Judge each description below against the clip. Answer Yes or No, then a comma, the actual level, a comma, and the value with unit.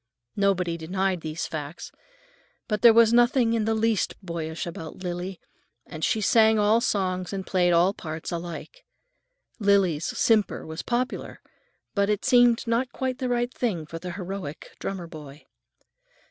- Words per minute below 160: Yes, average, 150 wpm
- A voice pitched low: No, high, 195 Hz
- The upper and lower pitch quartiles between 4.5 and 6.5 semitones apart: Yes, average, 5.0 semitones